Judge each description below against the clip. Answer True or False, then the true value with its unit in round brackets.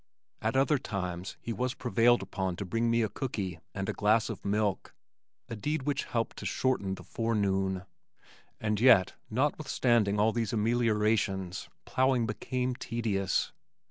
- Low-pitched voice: True (110 Hz)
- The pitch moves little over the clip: False (3.6 semitones)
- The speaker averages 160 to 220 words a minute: False (150 wpm)